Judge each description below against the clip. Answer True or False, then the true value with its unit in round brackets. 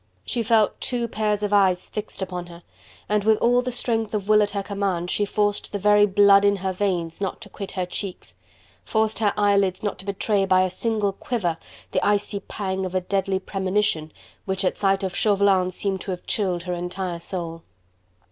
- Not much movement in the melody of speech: True (2.0 semitones)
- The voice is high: True (200 Hz)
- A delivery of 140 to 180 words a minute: False (200 wpm)